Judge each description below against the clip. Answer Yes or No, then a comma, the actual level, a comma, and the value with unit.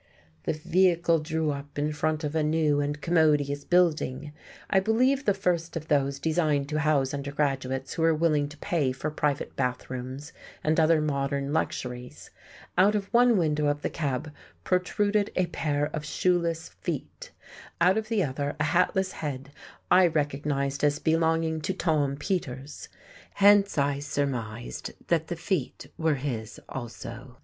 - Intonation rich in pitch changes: No, average, 3.2 semitones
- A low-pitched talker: No, medium, 150 Hz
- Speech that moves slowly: No, average, 155 wpm